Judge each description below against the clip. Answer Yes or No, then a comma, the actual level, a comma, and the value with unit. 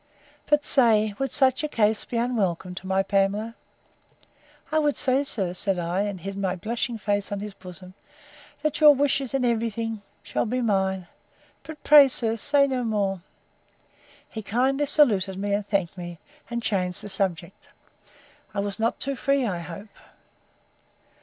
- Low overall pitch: No, high, 215 Hz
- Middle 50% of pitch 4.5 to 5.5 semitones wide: Yes, average, 4.8 semitones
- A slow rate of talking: No, average, 160 wpm